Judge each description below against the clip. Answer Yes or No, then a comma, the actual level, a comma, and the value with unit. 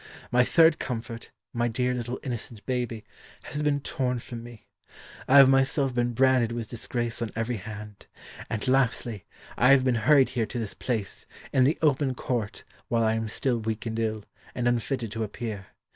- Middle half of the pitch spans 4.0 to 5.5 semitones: No, narrow, 2.5 semitones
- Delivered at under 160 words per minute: No, average, 180 wpm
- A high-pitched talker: No, low, 120 Hz